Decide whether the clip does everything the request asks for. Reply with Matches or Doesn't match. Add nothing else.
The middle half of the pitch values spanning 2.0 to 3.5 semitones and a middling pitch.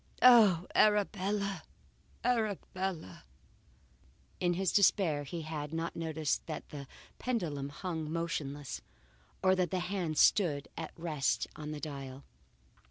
Doesn't match